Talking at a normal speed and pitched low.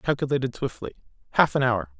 Yes: average, 180 wpm; low, 125 Hz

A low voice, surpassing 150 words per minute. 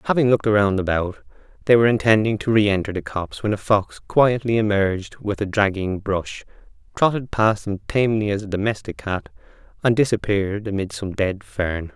Yes: low, 105 Hz; average, 170 wpm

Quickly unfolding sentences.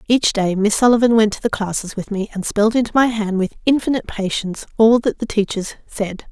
Yes: fast, 220 wpm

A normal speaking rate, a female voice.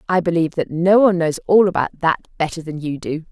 No: fast, 235 wpm; female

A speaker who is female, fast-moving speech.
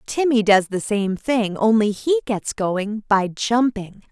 No: female; average, 160 wpm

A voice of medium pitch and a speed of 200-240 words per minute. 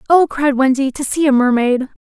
No: very high, 270 Hz; fast, 205 wpm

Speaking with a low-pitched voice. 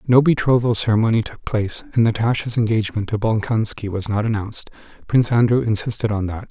Yes: low, 110 Hz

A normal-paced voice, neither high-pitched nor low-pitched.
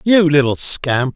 Yes: average, 155 wpm; medium, 150 Hz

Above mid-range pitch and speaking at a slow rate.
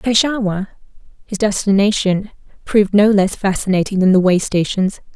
Yes: high, 200 Hz; slow, 130 wpm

